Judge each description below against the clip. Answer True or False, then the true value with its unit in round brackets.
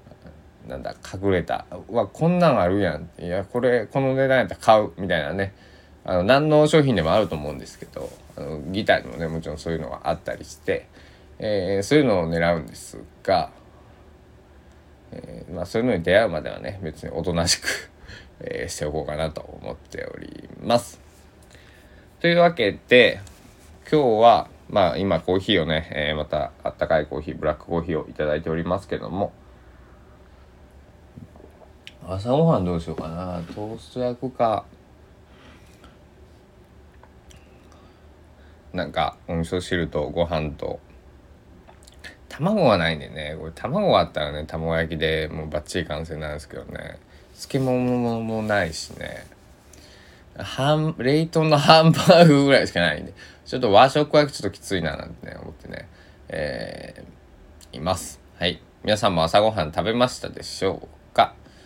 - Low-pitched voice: True (85 Hz)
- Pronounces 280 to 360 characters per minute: True (310 characters per minute)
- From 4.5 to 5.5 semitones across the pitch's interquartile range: True (5.2 semitones)